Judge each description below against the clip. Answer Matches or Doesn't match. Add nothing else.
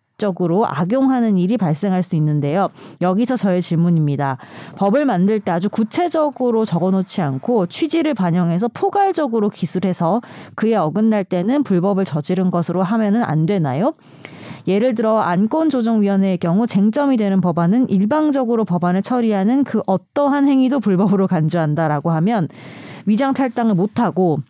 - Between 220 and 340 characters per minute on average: Doesn't match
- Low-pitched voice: Doesn't match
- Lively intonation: Doesn't match